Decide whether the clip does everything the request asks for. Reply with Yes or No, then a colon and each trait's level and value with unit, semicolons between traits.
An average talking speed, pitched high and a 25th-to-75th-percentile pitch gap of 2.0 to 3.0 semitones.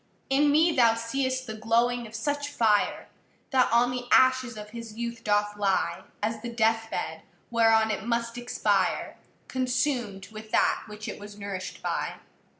Yes: average, 160 wpm; high, 230 Hz; narrow, 2.6 semitones